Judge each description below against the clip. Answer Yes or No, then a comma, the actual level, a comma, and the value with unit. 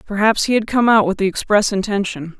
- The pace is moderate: No, fast, 225 wpm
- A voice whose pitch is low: No, high, 205 Hz